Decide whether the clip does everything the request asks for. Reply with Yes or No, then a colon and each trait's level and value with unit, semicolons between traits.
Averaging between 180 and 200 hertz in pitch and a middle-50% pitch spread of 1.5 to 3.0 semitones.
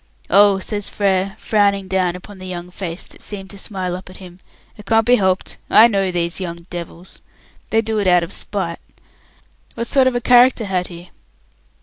Yes: high, 190 Hz; narrow, 2.6 semitones